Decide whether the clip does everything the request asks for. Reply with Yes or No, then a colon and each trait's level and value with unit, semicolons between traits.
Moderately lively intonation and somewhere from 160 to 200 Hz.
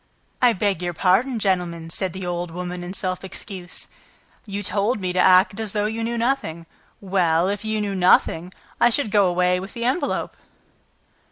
Yes: average, 3.1 semitones; high, 190 Hz